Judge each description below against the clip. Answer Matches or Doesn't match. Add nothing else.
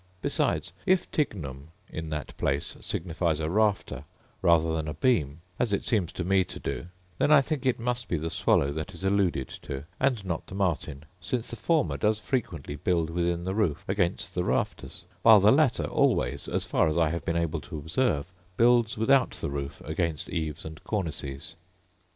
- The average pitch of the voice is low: Matches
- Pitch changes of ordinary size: Doesn't match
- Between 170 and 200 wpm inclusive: Matches